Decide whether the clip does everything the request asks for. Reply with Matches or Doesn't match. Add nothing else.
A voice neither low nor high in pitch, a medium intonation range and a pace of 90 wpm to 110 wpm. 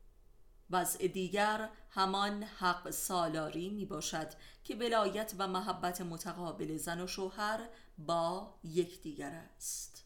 Matches